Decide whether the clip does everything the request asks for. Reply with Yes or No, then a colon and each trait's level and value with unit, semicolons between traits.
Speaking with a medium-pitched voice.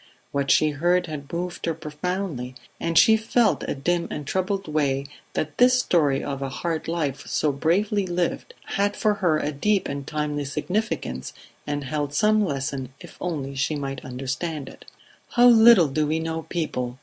Yes: medium, 155 Hz